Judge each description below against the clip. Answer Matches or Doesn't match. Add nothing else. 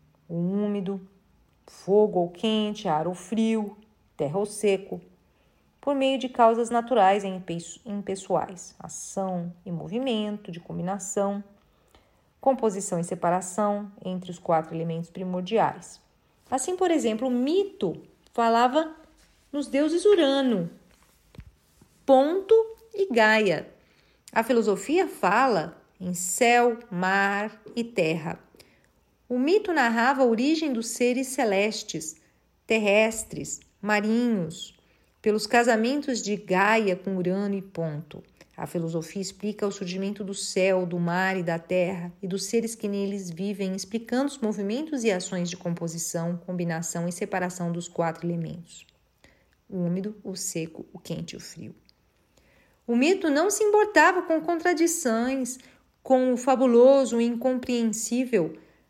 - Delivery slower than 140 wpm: Matches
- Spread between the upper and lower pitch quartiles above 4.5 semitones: Matches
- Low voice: Doesn't match